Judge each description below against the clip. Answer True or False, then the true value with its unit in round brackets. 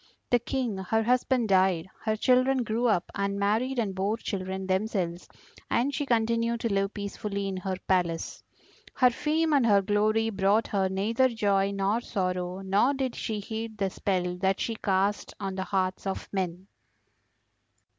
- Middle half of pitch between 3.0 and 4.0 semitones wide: True (3.3 semitones)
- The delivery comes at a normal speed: True (165 wpm)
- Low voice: False (205 Hz)